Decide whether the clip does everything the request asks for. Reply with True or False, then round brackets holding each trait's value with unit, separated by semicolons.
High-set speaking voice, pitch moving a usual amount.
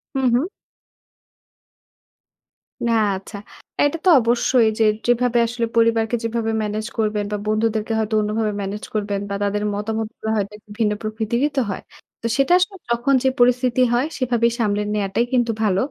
False (225 Hz; 2.2 semitones)